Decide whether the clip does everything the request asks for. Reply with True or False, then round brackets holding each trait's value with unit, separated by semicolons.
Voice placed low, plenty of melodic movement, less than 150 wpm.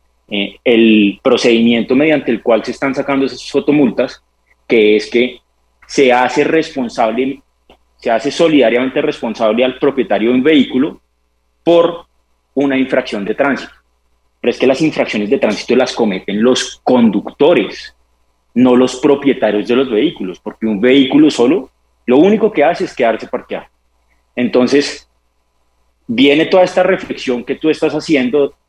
True (125 Hz; 6.2 semitones; 140 wpm)